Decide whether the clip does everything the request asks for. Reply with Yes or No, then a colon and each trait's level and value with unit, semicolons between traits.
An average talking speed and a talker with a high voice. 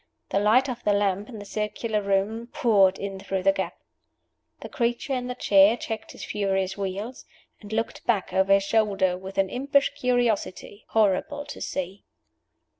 Yes: average, 170 wpm; high, 205 Hz